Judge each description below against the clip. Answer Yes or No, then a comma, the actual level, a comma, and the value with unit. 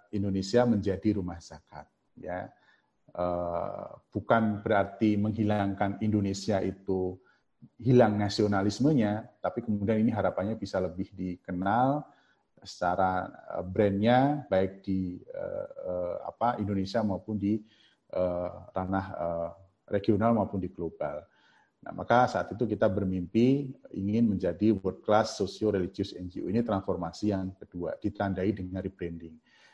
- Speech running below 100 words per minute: No, average, 105 wpm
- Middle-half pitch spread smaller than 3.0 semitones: Yes, narrow, 2.6 semitones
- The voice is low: Yes, low, 100 Hz